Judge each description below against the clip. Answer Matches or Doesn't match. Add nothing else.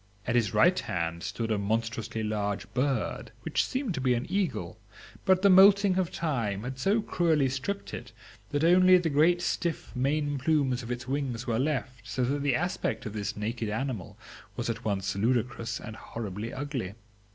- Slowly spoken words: Doesn't match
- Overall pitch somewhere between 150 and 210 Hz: Doesn't match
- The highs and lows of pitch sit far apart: Matches